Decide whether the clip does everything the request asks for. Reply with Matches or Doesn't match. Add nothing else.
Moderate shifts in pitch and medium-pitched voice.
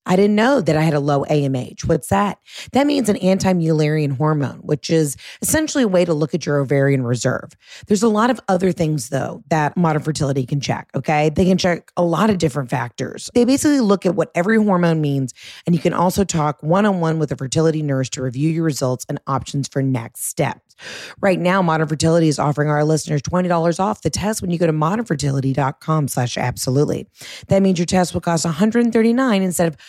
Matches